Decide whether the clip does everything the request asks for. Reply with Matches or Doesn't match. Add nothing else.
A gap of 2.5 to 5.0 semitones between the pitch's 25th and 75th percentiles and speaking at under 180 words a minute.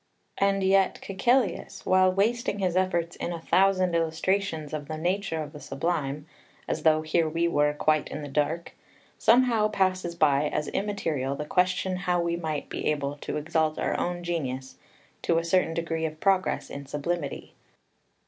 Matches